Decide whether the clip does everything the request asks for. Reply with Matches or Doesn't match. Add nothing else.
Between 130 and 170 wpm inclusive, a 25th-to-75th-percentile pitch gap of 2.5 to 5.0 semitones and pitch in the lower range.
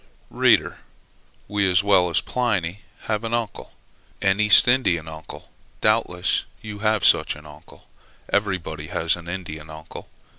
Matches